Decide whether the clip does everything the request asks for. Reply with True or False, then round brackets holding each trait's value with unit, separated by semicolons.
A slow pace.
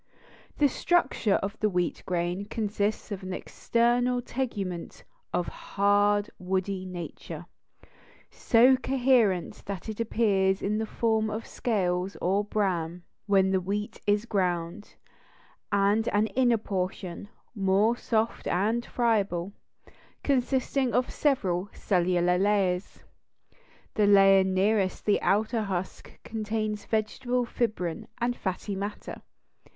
True (115 wpm)